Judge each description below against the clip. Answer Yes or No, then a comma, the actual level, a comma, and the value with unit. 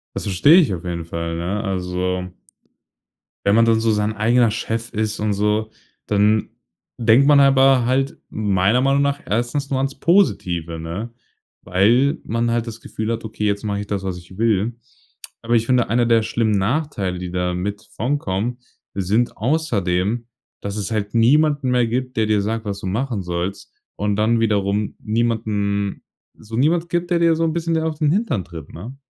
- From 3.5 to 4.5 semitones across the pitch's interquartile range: Yes, average, 4.1 semitones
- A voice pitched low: Yes, low, 110 Hz